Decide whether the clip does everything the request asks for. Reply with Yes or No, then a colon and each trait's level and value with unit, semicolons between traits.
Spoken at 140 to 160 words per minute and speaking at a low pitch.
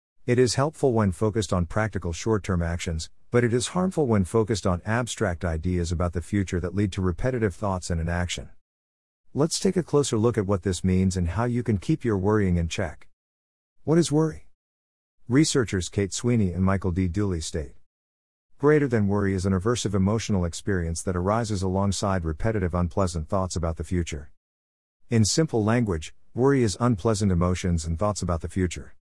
No: average, 180 wpm; very low, 95 Hz